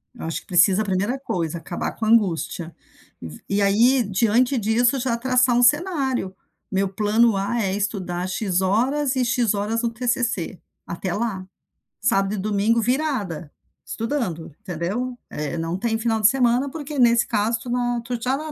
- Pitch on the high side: Yes, high, 225 Hz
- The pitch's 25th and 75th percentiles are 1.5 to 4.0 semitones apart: No, average, 4.4 semitones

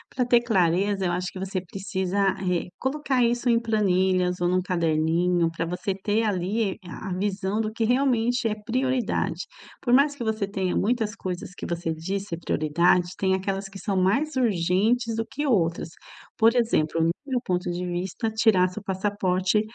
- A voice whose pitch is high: Yes, high, 195 Hz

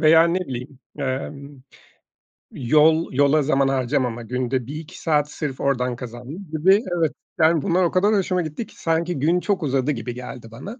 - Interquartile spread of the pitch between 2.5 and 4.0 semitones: No, average, 4.4 semitones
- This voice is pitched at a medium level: Yes, medium, 150 Hz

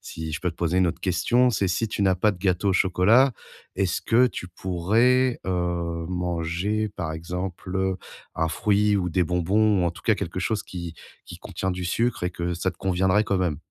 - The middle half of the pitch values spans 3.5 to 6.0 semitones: No, average, 2.8 semitones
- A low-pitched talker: Yes, very low, 90 Hz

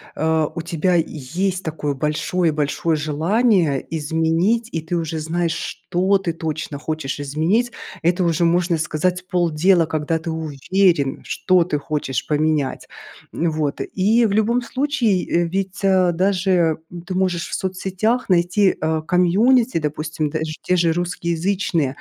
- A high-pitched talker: No, medium, 170 Hz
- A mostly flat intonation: No, average, 3.1 semitones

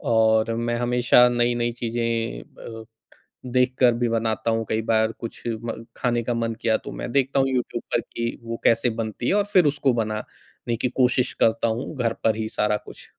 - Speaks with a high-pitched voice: No, low, 115 Hz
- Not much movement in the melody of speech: Yes, narrow, 1.6 semitones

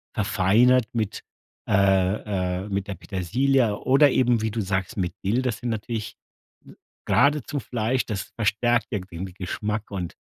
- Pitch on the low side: Yes, low, 105 Hz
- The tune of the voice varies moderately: Yes, average, 4.0 semitones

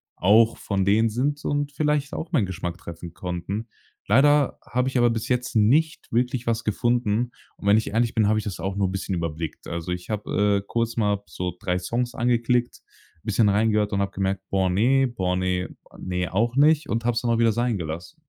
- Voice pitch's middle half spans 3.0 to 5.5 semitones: Yes, average, 4.1 semitones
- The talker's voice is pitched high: No, low, 110 Hz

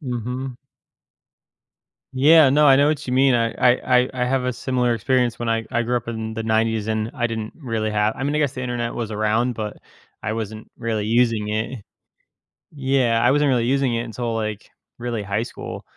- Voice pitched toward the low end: Yes, low, 120 Hz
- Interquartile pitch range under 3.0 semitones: Yes, narrow, 2.5 semitones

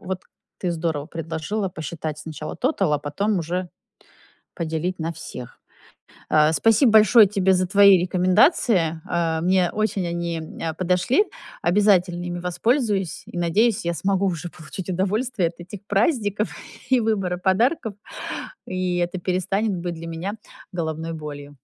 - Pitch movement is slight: No, average, 3.3 semitones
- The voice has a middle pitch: Yes, medium, 180 Hz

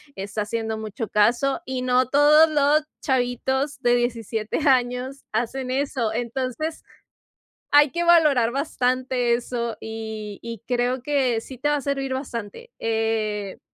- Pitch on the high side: Yes, very high, 250 Hz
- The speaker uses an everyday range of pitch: Yes, average, 3.4 semitones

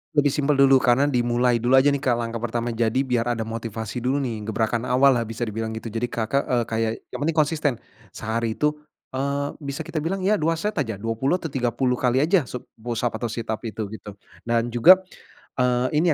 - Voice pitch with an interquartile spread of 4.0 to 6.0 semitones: No, average, 3.4 semitones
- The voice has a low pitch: Yes, low, 125 Hz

